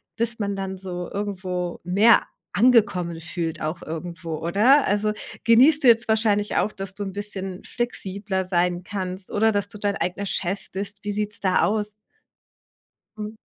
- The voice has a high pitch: Yes, high, 200 Hz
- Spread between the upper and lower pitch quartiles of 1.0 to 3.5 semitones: Yes, narrow, 2.6 semitones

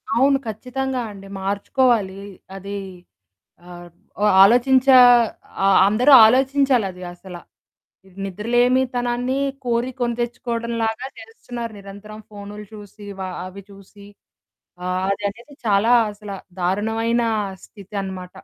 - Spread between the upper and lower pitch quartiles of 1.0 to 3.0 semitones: No, average, 3.6 semitones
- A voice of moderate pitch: No, high, 220 Hz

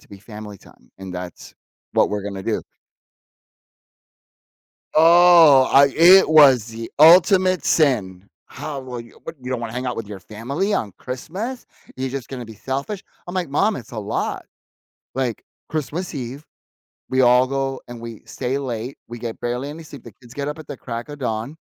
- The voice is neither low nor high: No, low, 130 Hz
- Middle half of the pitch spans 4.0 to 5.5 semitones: Yes, average, 4.8 semitones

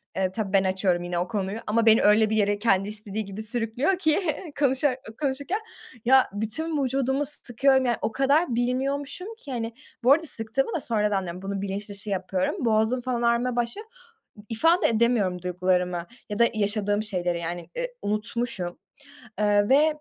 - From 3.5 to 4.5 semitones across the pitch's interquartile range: No, average, 4.9 semitones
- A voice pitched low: No, high, 225 Hz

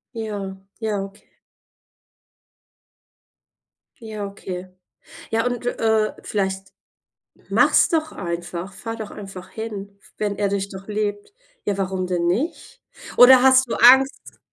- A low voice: No, high, 205 Hz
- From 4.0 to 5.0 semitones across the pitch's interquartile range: No, average, 2.9 semitones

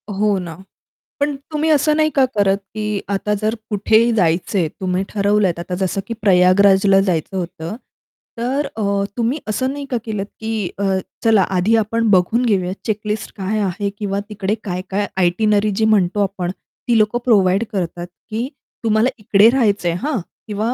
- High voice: Yes, high, 205 Hz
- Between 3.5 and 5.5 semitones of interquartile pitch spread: No, average, 2.8 semitones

